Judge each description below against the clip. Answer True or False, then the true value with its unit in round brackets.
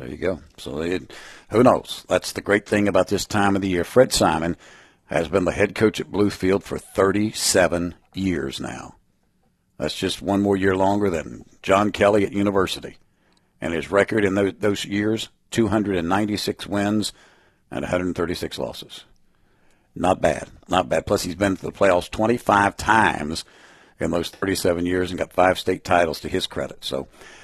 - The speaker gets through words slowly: False (170 wpm)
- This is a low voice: True (95 Hz)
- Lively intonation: False (2.5 semitones)